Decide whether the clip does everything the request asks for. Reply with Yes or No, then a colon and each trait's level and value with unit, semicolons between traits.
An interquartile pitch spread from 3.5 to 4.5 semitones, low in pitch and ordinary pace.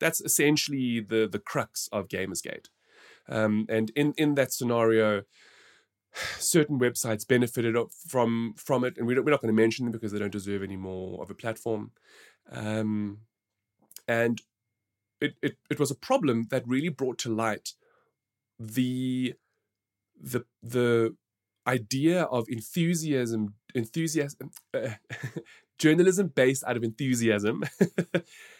No: average, 4.2 semitones; low, 120 Hz; slow, 130 wpm